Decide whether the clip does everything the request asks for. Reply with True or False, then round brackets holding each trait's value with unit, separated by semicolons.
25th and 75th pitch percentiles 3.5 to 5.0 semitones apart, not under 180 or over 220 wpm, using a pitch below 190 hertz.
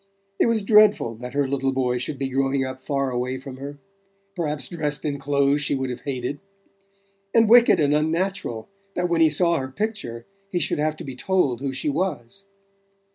True (4.4 semitones; 190 wpm; 140 Hz)